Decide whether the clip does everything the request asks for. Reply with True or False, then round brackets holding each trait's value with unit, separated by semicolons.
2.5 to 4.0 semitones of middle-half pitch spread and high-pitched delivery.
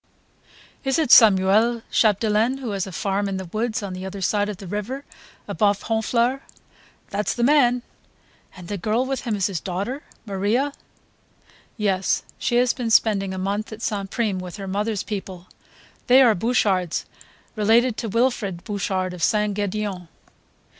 True (3.4 semitones; 210 Hz)